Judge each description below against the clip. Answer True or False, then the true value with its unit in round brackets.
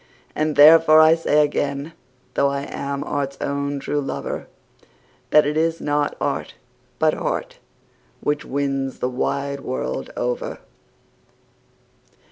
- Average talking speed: False (120 wpm)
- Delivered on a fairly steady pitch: True (1.7 semitones)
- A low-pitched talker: False (145 Hz)